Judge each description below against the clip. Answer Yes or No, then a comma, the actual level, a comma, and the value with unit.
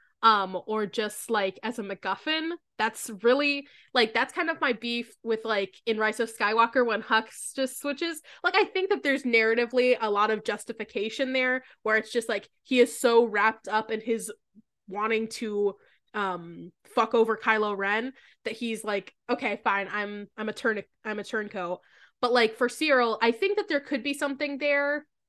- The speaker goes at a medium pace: Yes, average, 185 wpm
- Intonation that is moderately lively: Yes, average, 3.4 semitones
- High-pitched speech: Yes, high, 230 Hz